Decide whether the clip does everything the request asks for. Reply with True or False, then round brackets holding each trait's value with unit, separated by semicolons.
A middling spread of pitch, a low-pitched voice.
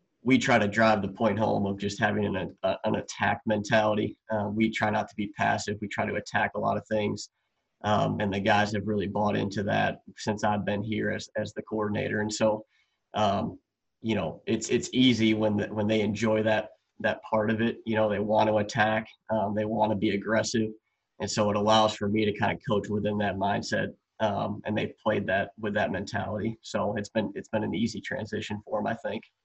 False (0.9 semitones; 105 Hz)